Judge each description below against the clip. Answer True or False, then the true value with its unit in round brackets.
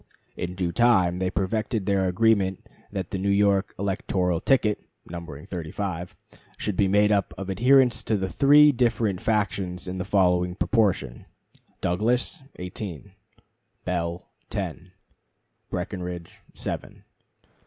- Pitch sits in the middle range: False (95 Hz)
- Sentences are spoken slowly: True (125 wpm)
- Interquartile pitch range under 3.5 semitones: True (2.8 semitones)